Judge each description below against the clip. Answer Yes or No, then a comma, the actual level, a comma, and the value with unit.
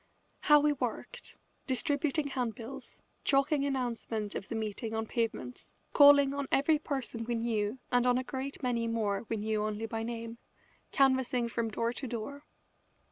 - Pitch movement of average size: Yes, average, 3.6 semitones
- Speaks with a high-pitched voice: Yes, high, 240 Hz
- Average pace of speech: Yes, average, 155 wpm